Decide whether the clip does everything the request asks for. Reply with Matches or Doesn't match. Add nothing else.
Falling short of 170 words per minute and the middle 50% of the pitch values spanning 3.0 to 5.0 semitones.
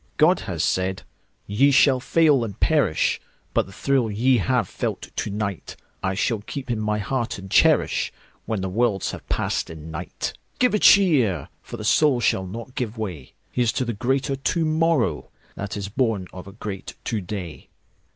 Doesn't match